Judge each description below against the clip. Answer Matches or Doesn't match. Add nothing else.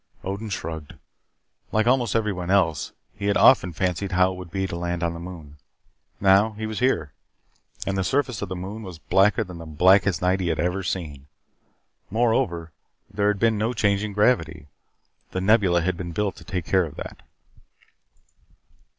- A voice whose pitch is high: Doesn't match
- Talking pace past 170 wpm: Matches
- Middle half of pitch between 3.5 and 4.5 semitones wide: Doesn't match